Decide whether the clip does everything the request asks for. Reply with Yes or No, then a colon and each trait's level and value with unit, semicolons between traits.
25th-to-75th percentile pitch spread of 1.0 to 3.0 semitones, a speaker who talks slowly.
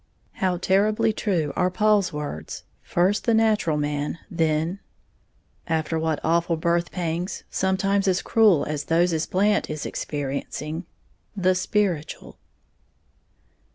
No: average, 3.8 semitones; slow, 115 wpm